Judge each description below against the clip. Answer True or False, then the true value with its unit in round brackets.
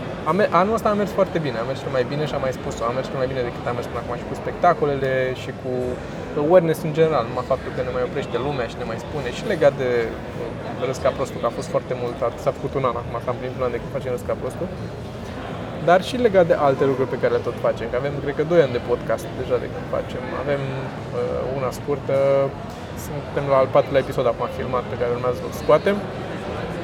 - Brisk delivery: True (230 wpm)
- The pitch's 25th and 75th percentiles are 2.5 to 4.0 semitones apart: True (3.5 semitones)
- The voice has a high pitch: False (135 Hz)